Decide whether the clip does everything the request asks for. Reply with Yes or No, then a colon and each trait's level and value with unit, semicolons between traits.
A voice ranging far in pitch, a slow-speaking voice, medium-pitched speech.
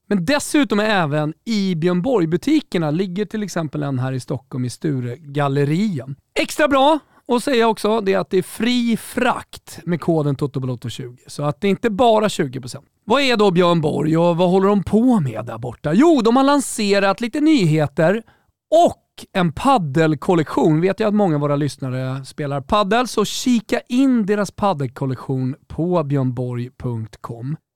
No: wide, 7.3 semitones; average, 165 wpm; medium, 175 Hz